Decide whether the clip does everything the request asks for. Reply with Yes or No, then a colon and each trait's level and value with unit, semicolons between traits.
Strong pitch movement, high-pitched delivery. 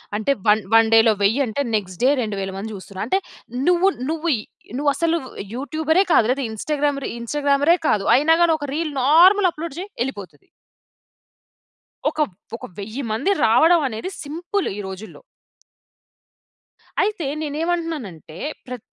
Yes: wide, 6.9 semitones; very high, 285 Hz